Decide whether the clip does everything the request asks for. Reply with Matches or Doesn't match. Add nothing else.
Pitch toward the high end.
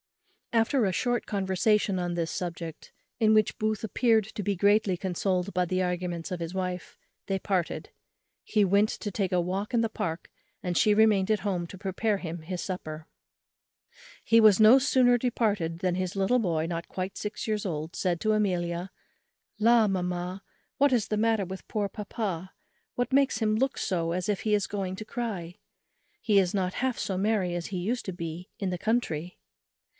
Matches